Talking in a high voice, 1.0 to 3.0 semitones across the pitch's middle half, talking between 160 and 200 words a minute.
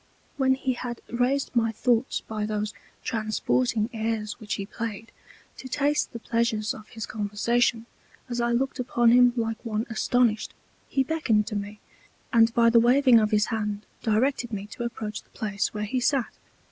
Yes: high, 230 Hz; narrow, 2.4 semitones; average, 170 wpm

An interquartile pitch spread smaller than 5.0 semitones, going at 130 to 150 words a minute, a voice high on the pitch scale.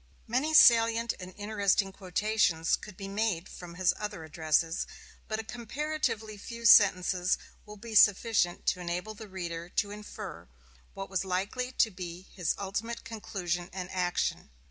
Yes: average, 3.5 semitones; average, 145 wpm; high, 200 Hz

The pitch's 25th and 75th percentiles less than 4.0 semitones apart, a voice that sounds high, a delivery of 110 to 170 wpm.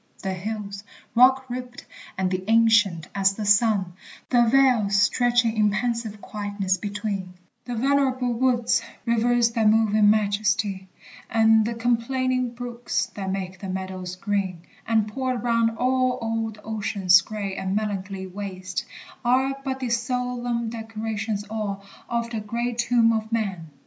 Yes: average, 3.2 semitones; high, 220 Hz; average, 140 wpm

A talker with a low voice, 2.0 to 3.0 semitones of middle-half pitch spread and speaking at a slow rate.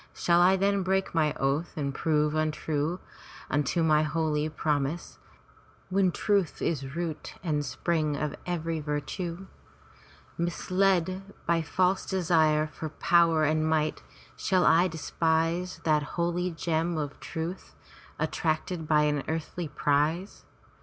No: medium, 160 Hz; narrow, 2.5 semitones; slow, 125 wpm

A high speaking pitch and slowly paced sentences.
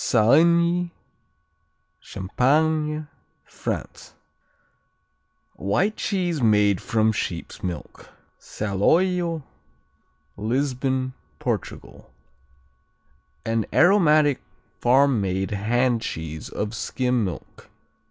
No: low, 125 Hz; slow, 70 wpm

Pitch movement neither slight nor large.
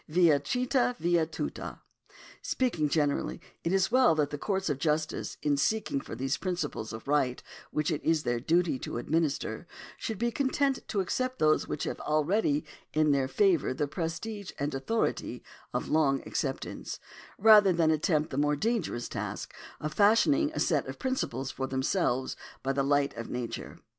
No: wide, 6.2 semitones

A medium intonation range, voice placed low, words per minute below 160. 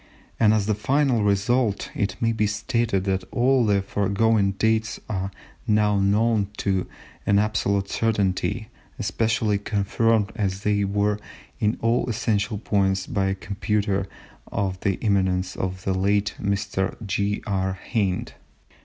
No: narrow, 2.1 semitones; low, 100 Hz; slow, 135 wpm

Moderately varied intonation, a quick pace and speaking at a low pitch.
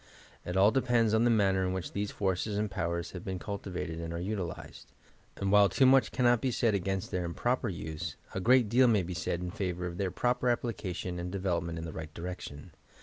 Yes: average, 4.0 semitones; fast, 220 wpm; very low, 95 Hz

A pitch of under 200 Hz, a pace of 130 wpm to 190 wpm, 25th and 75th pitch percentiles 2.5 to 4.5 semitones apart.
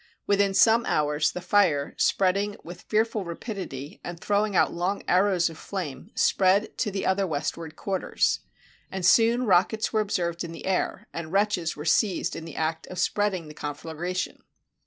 Yes: medium, 185 Hz; average, 170 wpm; average, 3.6 semitones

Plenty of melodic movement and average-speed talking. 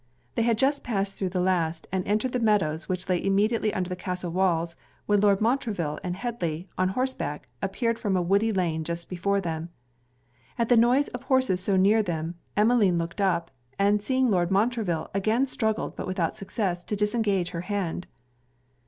No: average, 3.9 semitones; average, 180 wpm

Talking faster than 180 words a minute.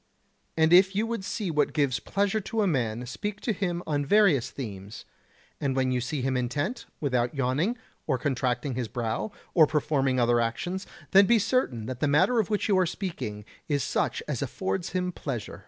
Yes: average, 190 wpm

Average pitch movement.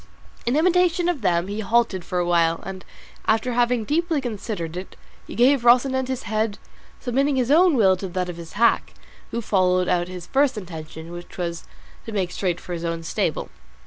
No: wide, 6.3 semitones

